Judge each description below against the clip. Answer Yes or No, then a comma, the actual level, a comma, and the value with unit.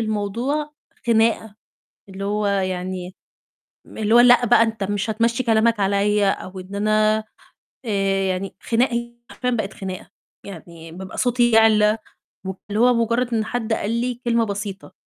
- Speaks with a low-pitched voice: No, high, 215 Hz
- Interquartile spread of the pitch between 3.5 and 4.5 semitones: No, average, 2.9 semitones